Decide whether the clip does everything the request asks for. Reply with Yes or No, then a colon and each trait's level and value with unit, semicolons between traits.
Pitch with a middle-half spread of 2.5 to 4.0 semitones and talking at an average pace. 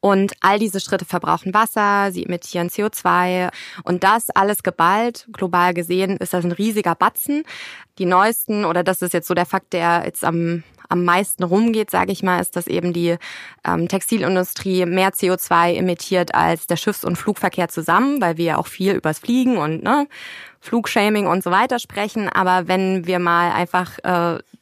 Yes: average, 2.8 semitones; average, 180 wpm